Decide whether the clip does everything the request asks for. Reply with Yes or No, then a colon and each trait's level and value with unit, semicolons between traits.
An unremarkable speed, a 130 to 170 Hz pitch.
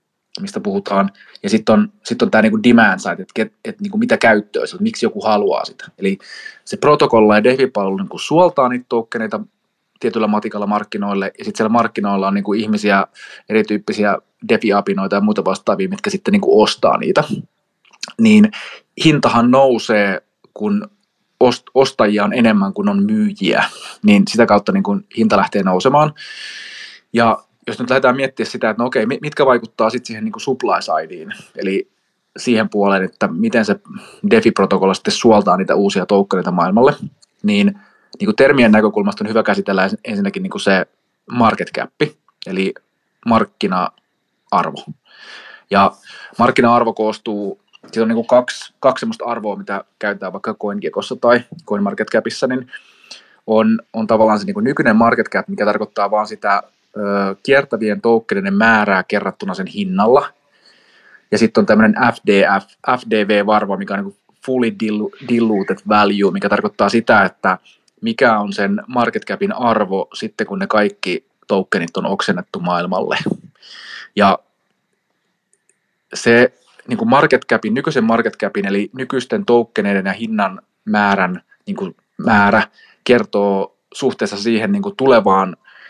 No: average, 140 wpm; low, 120 Hz